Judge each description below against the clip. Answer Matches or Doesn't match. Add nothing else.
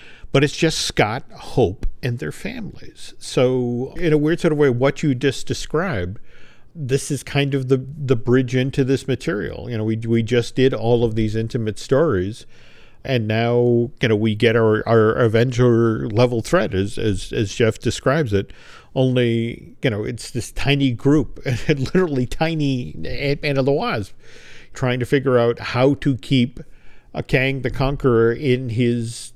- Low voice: Matches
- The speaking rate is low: Doesn't match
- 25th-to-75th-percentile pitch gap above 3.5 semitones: Doesn't match